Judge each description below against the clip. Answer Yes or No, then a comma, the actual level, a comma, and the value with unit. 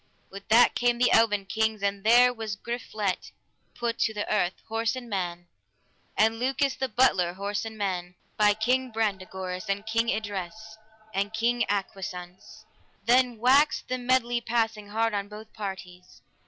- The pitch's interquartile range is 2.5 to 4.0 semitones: Yes, average, 3.1 semitones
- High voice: Yes, high, 220 Hz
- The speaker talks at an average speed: Yes, average, 155 wpm